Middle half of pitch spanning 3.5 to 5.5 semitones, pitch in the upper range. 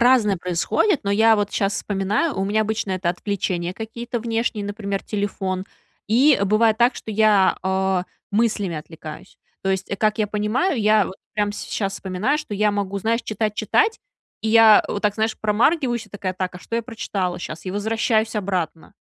No: average, 2.7 semitones; high, 210 Hz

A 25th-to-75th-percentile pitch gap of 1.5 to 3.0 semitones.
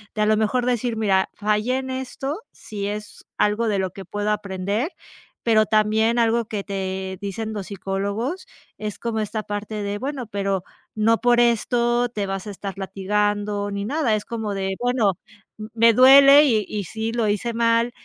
Yes: average, 2.7 semitones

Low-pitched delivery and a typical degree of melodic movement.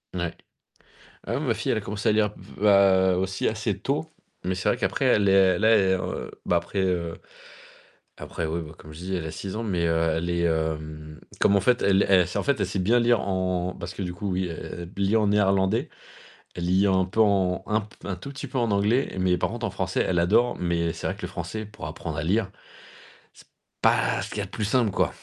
Yes: very low, 95 Hz; average, 3.2 semitones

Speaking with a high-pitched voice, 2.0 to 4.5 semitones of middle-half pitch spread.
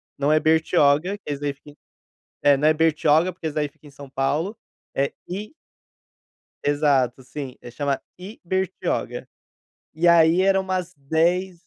No: medium, 155 Hz; average, 4.0 semitones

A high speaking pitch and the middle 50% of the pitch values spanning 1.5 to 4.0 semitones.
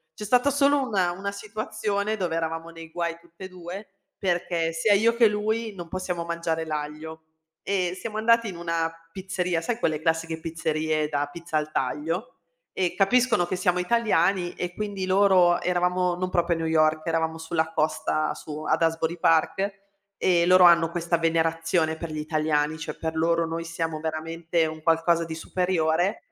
No: medium, 170 Hz; narrow, 2.6 semitones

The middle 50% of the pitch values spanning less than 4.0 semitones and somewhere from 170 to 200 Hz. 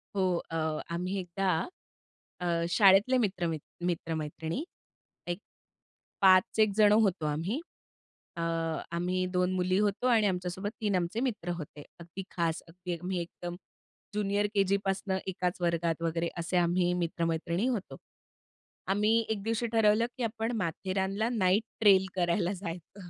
Yes: average, 3.0 semitones; medium, 185 Hz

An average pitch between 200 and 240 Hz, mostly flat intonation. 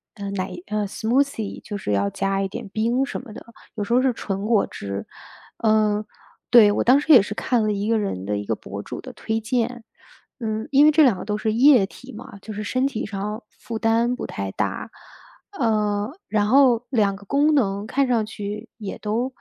No: high, 220 Hz; average, 3.3 semitones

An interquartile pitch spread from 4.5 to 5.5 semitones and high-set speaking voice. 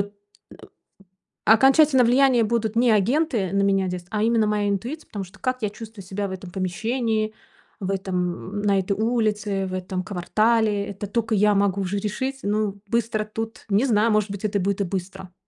No: narrow, 2.6 semitones; high, 210 Hz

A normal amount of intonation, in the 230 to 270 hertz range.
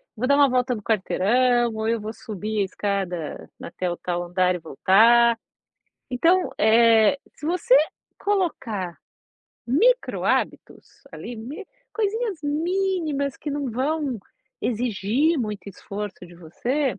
No: wide, 6.1 semitones; high, 235 Hz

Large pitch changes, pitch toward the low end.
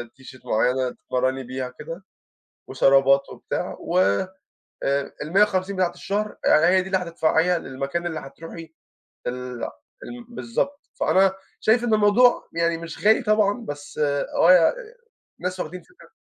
No: wide, 6.3 semitones; medium, 170 Hz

